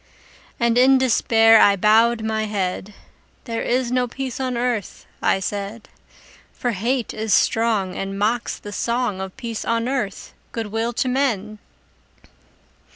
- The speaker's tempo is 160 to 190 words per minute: No, average, 145 wpm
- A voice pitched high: Yes, high, 225 Hz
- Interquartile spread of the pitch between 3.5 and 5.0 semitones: No, average, 2.8 semitones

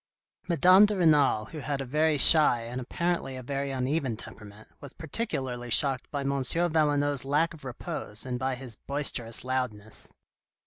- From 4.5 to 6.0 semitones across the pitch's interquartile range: No, average, 3.7 semitones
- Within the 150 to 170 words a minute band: Yes, average, 160 wpm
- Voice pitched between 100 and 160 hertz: Yes, low, 135 Hz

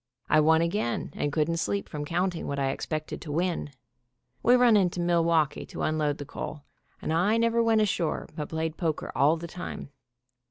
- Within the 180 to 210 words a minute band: Yes, average, 185 wpm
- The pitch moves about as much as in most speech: Yes, average, 3.1 semitones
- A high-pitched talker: No, medium, 165 Hz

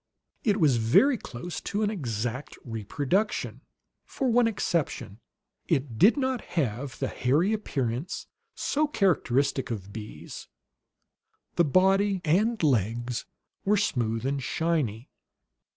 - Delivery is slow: Yes, slow, 115 wpm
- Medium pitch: Yes, medium, 145 Hz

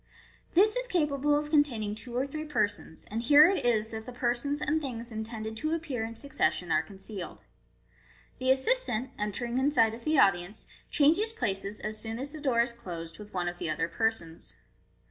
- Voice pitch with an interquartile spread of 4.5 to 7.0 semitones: Yes, wide, 5.4 semitones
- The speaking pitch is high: Yes, high, 240 Hz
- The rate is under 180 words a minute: No, average, 195 wpm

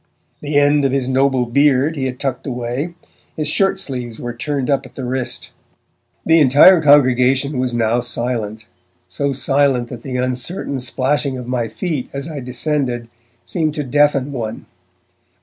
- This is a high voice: No, low, 130 Hz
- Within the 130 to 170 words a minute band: Yes, average, 160 wpm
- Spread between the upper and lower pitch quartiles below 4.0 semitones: Yes, average, 2.7 semitones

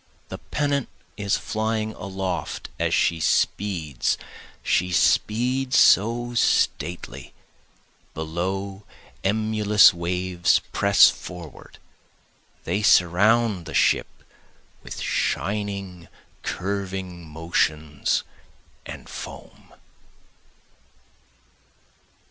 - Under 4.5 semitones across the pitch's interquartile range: Yes, average, 3.7 semitones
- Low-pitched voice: Yes, very low, 95 Hz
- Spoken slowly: Yes, slow, 75 wpm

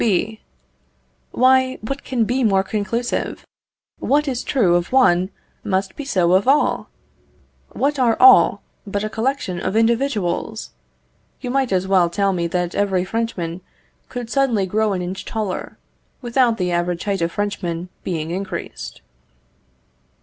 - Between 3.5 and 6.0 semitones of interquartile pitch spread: Yes, average, 5.2 semitones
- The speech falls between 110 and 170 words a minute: Yes, average, 140 wpm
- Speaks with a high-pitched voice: Yes, high, 205 Hz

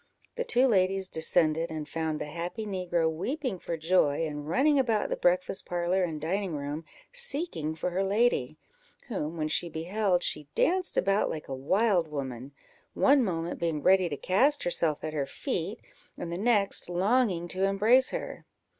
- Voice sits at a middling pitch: Yes, medium, 175 Hz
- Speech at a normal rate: Yes, average, 170 wpm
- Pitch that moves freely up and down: No, average, 4.7 semitones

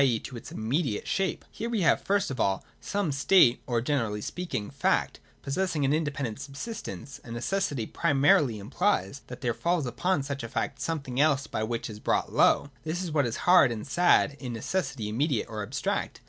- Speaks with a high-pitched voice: No, medium, 140 Hz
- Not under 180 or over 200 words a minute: Yes, average, 190 wpm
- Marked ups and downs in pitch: Yes, wide, 5.8 semitones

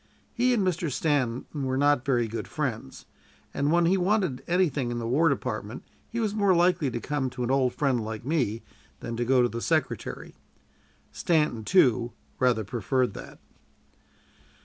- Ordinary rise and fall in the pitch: No, wide, 5.7 semitones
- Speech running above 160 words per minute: Yes, average, 170 wpm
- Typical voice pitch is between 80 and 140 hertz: Yes, low, 135 Hz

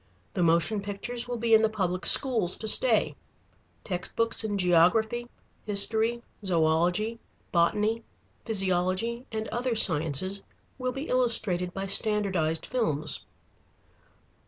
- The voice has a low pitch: No, high, 210 Hz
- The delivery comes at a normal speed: No, slow, 115 wpm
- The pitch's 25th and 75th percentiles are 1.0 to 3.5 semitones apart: No, average, 4.3 semitones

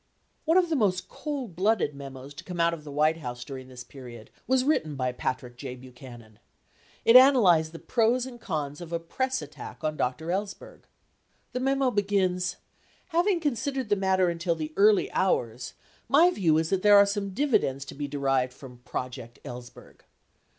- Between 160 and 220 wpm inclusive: Yes, average, 180 wpm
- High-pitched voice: No, medium, 170 Hz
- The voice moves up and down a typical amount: No, wide, 8.6 semitones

